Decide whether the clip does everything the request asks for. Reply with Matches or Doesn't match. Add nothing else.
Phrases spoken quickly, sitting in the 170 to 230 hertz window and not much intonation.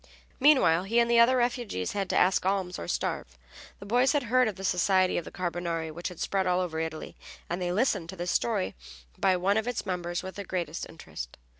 Doesn't match